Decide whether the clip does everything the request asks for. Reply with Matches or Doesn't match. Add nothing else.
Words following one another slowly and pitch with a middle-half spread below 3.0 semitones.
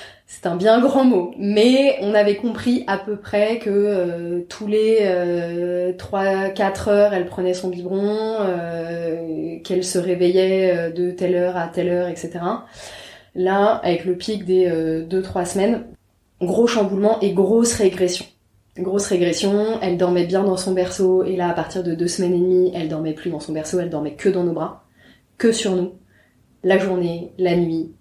Doesn't match